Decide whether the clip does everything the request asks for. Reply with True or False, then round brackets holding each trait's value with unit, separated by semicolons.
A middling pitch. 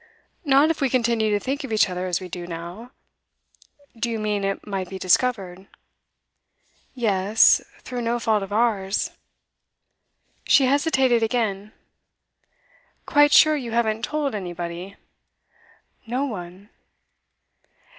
False (220 Hz)